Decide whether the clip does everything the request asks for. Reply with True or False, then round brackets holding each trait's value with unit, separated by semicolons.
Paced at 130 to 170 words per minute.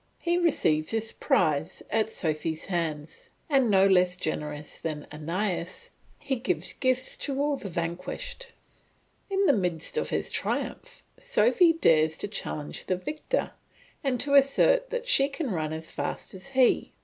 True (150 wpm)